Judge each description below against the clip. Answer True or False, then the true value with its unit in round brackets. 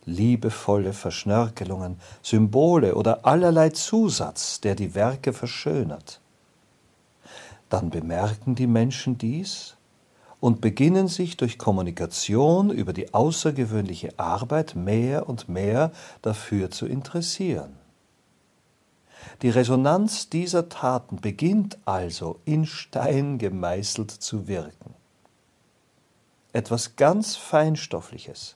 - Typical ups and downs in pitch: False (7.3 semitones)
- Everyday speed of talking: False (90 wpm)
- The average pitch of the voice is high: False (120 Hz)